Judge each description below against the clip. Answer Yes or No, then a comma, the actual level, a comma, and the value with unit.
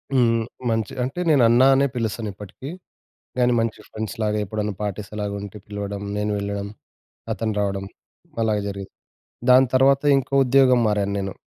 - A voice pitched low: Yes, low, 105 Hz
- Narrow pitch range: No, average, 3.3 semitones